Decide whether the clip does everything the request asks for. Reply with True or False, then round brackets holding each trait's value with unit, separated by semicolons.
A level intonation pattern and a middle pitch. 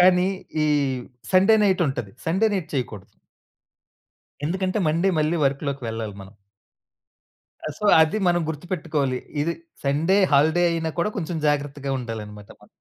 False (4.5 semitones; 155 Hz)